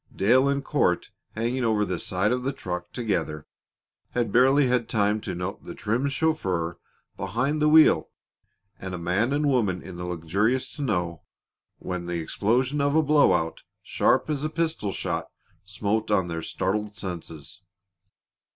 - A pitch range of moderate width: No, wide, 6.8 semitones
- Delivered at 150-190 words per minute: Yes, average, 155 wpm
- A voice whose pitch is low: Yes, low, 105 Hz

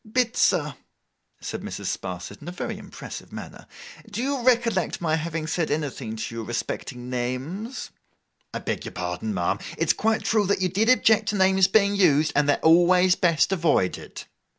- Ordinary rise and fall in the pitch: No, wide, 7.1 semitones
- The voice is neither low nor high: Yes, medium, 175 Hz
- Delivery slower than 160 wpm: No, average, 170 wpm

